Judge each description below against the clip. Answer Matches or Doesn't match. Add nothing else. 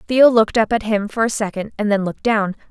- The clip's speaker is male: Doesn't match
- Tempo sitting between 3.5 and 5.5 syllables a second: Doesn't match